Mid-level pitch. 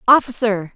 No: high, 225 Hz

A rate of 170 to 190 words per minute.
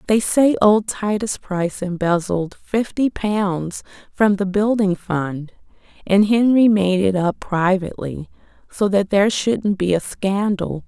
No: average, 140 wpm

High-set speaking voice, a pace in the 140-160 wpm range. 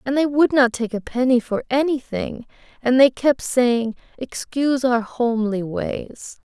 Yes: very high, 250 Hz; average, 155 wpm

